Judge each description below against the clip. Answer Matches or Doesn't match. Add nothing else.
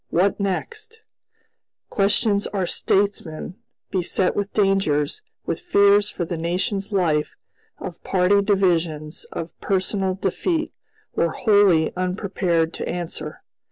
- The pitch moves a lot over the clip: Doesn't match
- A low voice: Doesn't match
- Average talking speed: Doesn't match